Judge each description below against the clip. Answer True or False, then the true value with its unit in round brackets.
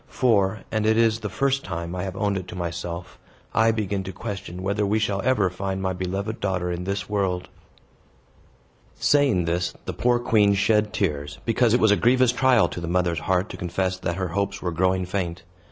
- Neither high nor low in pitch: False (95 Hz)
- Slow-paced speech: False (200 wpm)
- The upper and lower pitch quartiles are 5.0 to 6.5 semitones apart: False (3.2 semitones)